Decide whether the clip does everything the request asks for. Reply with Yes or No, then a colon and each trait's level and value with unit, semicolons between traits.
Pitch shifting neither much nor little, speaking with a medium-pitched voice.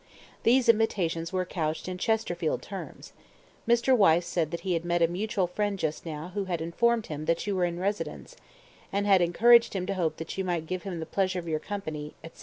Yes: average, 3.6 semitones; medium, 180 Hz